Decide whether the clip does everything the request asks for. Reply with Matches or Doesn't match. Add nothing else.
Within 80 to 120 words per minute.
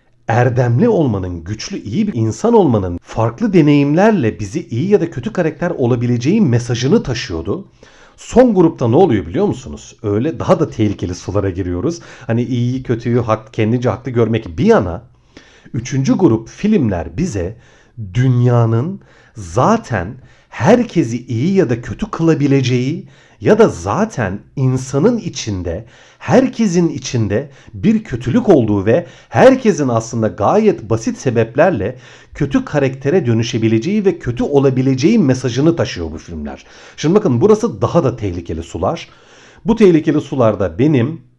Doesn't match